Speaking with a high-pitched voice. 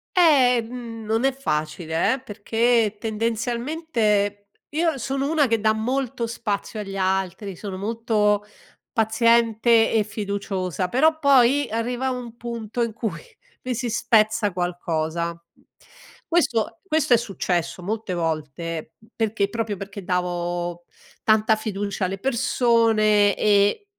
Yes: high, 220 Hz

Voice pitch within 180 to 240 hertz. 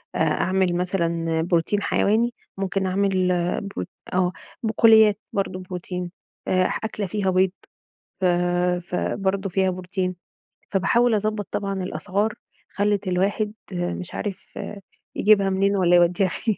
Yes: high, 190 Hz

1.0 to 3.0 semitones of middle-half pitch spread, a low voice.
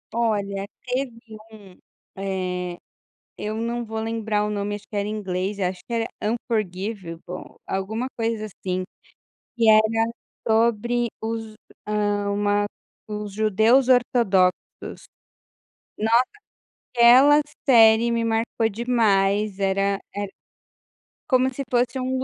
No: average, 2.7 semitones; high, 215 Hz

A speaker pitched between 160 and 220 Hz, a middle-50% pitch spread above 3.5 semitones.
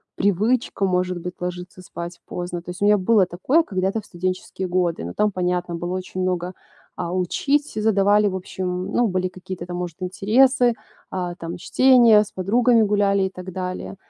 No: medium, 185 Hz; average, 2.7 semitones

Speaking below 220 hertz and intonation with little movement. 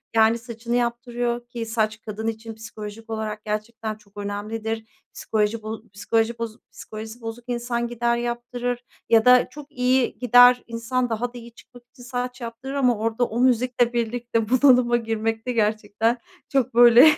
No: high, 235 Hz; narrow, 1.7 semitones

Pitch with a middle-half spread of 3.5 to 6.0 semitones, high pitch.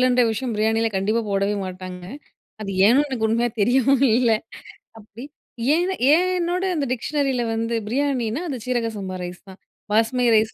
Yes: average, 4.1 semitones; high, 235 Hz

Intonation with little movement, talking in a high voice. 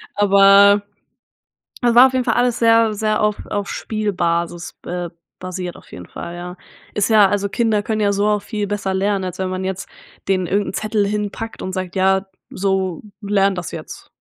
Yes: narrow, 2.1 semitones; high, 200 Hz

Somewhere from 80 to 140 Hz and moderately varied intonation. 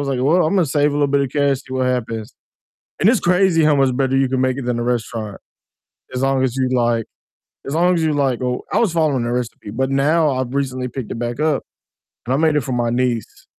Yes: low, 135 Hz; average, 3.0 semitones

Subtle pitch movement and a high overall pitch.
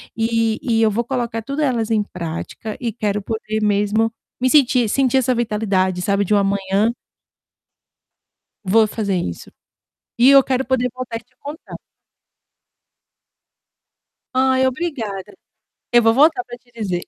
No: average, 3.5 semitones; high, 225 Hz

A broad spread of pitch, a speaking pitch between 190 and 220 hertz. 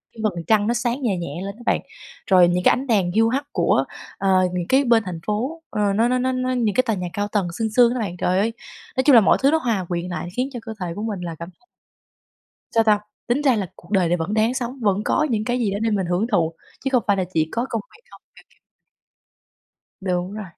No: average, 4.8 semitones; high, 215 Hz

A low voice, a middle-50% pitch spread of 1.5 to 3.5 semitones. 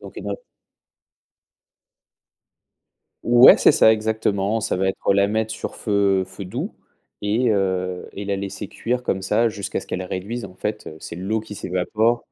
Yes: low, 100 Hz; narrow, 2.6 semitones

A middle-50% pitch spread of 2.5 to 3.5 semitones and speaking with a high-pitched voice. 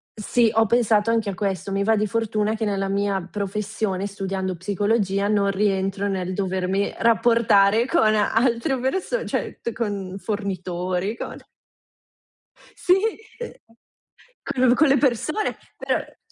Yes: average, 2.8 semitones; high, 205 Hz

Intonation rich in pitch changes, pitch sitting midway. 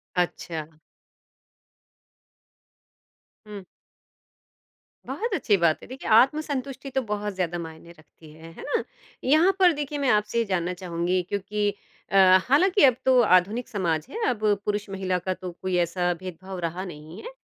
No: wide, 6.5 semitones; high, 195 Hz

